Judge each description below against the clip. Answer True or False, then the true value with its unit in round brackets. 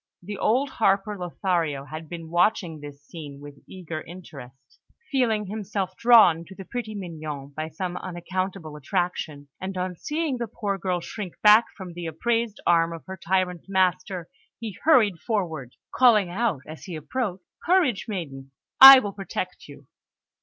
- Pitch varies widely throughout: False (4.5 semitones)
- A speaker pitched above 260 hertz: False (185 Hz)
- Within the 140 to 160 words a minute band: True (155 wpm)